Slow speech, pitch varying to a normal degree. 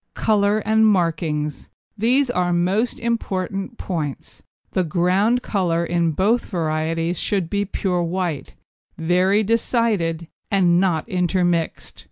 Yes: slow, 115 wpm; average, 3.6 semitones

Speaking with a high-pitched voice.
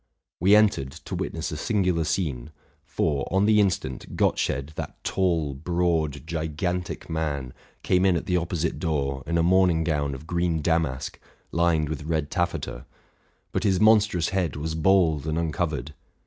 No: very low, 80 Hz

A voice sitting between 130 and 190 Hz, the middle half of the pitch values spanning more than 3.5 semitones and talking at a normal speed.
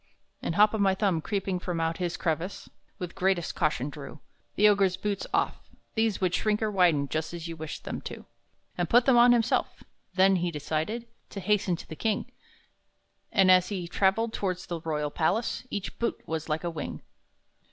Yes: medium, 185 Hz; average, 4.0 semitones; average, 190 wpm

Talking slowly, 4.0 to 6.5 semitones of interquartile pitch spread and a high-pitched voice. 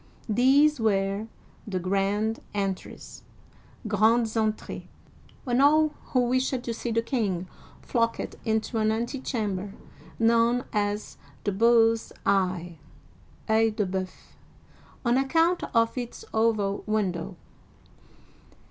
No: slow, 110 wpm; average, 3.1 semitones; high, 220 Hz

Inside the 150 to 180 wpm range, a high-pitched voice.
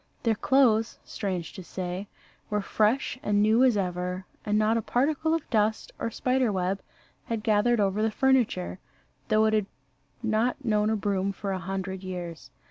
Yes: average, 170 wpm; high, 210 Hz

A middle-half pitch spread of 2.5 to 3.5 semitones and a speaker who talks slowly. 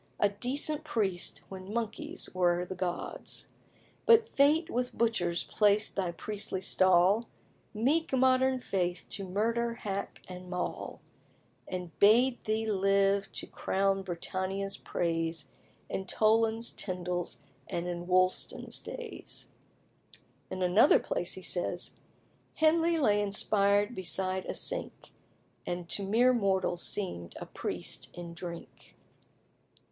No: average, 4.3 semitones; slow, 120 wpm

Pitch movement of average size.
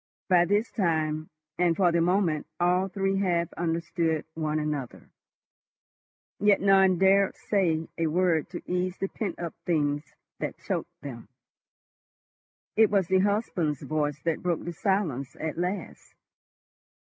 Yes: average, 3.4 semitones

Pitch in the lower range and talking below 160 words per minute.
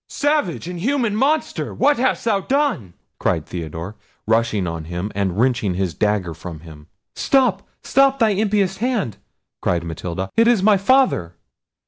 Yes: low, 130 Hz; average, 145 wpm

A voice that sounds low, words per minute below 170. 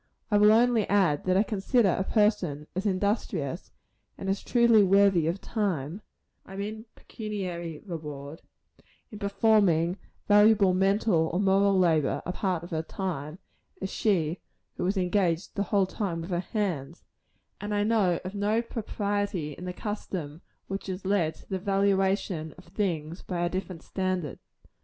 No: high, 190 Hz; average, 155 wpm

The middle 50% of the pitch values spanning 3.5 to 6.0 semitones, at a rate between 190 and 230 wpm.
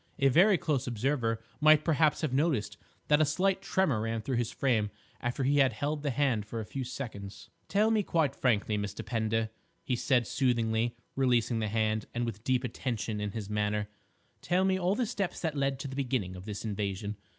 Yes: average, 5.2 semitones; average, 200 wpm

